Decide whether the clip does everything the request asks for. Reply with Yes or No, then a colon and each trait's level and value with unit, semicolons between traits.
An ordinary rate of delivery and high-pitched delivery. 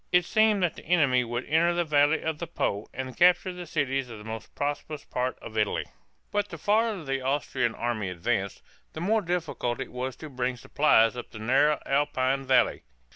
No: average, 195 wpm; medium, 140 Hz